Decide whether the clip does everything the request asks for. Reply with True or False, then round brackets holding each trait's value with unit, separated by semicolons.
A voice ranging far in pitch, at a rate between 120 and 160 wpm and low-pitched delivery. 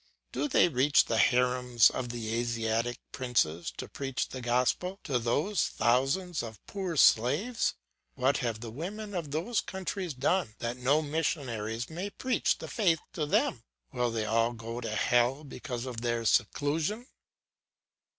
True (5.8 semitones; 150 wpm; 125 Hz)